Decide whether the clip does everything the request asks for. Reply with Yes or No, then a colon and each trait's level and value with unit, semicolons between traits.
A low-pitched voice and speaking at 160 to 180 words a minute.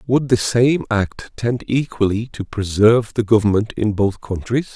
Yes: low, 110 Hz; average, 165 wpm